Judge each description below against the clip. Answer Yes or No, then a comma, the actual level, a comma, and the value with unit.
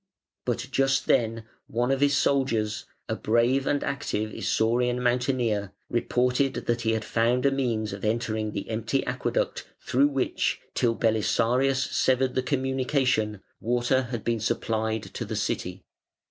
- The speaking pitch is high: No, low, 120 Hz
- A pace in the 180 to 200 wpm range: No, average, 145 wpm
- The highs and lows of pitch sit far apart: No, average, 2.9 semitones